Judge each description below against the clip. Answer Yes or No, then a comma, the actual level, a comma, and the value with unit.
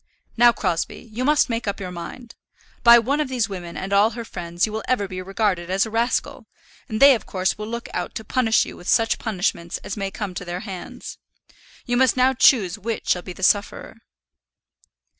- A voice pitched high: Yes, high, 215 Hz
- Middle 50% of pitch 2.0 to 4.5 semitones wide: Yes, average, 4.2 semitones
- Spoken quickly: Yes, fast, 210 wpm